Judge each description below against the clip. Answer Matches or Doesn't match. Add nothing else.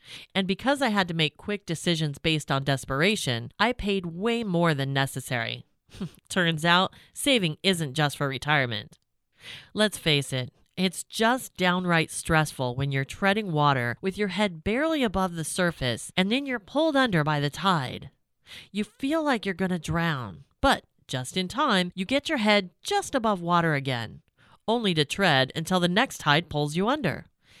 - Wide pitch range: Matches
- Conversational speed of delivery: Matches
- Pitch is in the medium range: Matches